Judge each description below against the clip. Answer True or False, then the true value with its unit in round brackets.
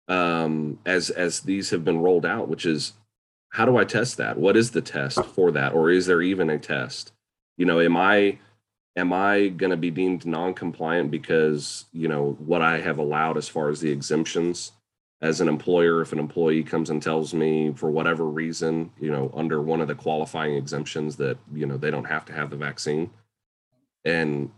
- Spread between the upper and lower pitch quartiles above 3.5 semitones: False (2.8 semitones)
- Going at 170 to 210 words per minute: True (205 wpm)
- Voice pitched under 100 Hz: True (80 Hz)